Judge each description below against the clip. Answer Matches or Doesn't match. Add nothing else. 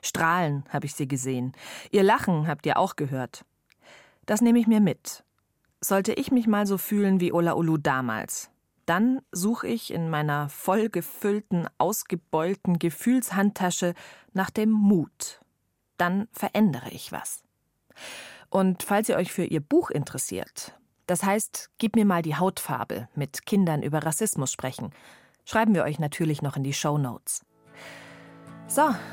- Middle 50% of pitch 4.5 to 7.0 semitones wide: Matches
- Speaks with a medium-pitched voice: Matches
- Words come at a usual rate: Matches